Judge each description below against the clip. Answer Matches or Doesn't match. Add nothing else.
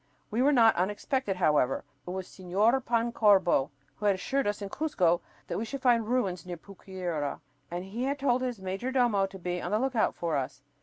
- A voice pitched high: Matches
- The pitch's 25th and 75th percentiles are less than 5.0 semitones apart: Doesn't match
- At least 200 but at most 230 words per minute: Matches